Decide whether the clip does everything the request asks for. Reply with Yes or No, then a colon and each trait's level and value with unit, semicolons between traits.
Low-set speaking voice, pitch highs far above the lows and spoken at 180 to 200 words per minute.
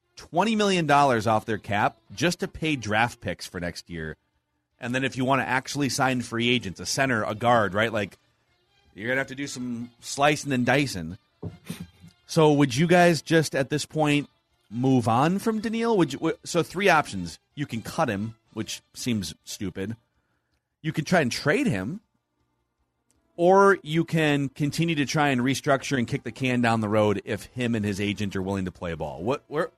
Yes: low, 125 Hz; wide, 5.9 semitones; average, 195 wpm